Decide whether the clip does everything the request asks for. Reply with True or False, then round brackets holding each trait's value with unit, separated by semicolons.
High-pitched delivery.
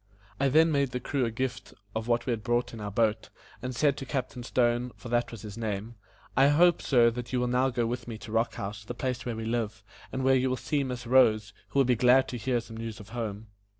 False (120 Hz)